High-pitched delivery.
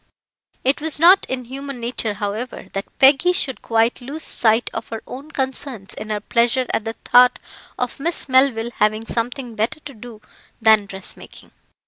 Yes: high, 245 Hz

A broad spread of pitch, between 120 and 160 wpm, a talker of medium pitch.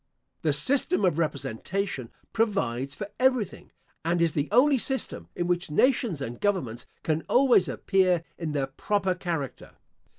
Yes: wide, 6.1 semitones; average, 140 wpm; medium, 175 Hz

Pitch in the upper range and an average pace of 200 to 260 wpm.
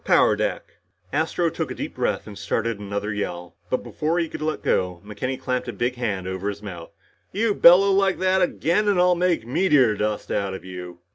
No: low, 120 Hz; fast, 205 wpm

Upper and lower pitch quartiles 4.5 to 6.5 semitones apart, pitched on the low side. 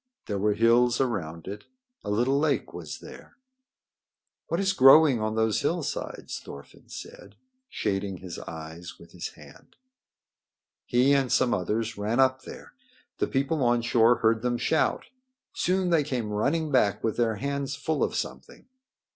Yes: average, 5.0 semitones; low, 120 Hz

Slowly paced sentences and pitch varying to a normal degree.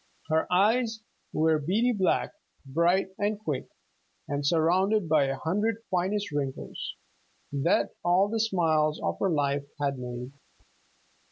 No: slow, 125 wpm; wide, 6.0 semitones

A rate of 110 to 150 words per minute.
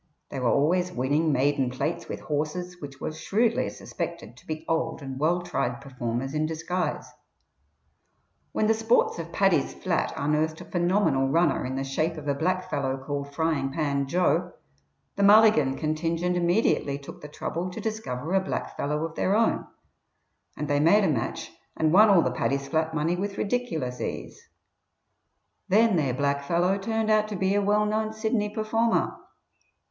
No: average, 165 wpm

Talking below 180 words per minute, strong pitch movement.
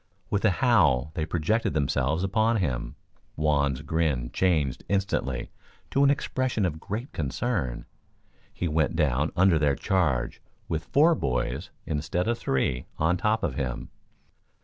Yes: average, 140 wpm; wide, 6.2 semitones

